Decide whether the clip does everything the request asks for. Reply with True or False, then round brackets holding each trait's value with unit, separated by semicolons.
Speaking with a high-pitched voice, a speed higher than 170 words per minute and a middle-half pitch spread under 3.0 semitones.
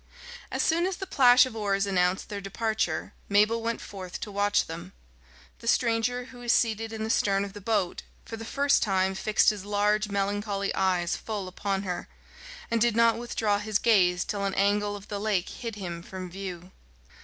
True (205 Hz; 190 wpm; 2.6 semitones)